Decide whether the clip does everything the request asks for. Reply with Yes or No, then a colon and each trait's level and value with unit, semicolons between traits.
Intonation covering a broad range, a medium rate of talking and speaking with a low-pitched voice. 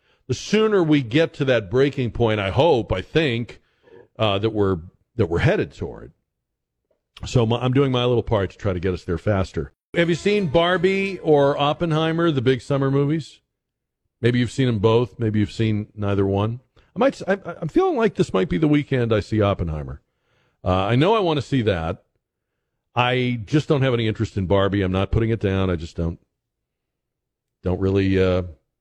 Yes: wide, 7.0 semitones; average, 195 wpm; low, 120 Hz